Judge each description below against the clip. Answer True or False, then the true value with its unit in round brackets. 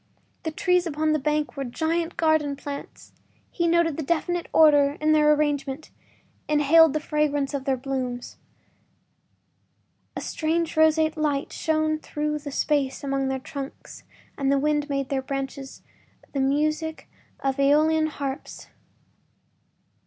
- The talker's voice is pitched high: True (300 Hz)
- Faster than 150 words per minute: False (140 wpm)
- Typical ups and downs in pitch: False (2.2 semitones)